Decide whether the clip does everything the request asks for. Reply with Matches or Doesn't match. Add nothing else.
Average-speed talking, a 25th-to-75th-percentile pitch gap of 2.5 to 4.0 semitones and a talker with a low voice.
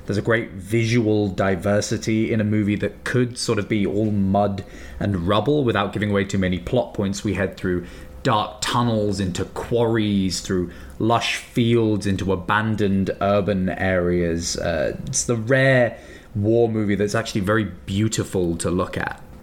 Matches